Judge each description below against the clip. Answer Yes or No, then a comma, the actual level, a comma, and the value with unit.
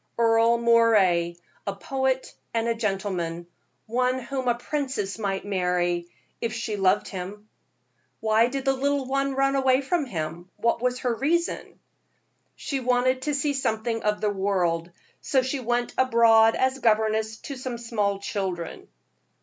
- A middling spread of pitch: Yes, average, 4.5 semitones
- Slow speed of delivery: No, average, 150 wpm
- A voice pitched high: Yes, high, 230 Hz